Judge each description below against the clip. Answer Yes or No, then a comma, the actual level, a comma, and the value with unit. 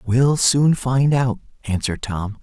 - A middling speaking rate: Yes, average, 150 wpm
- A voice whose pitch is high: No, low, 125 Hz